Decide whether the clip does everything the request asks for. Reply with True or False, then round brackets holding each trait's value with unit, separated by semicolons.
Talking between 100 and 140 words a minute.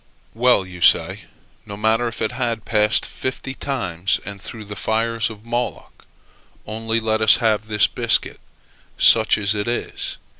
False (155 wpm)